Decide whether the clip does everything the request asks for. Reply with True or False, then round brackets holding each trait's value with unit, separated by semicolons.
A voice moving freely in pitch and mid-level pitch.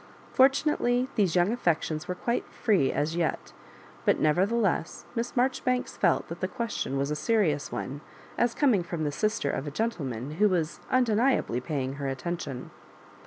True (7.8 semitones; 175 Hz)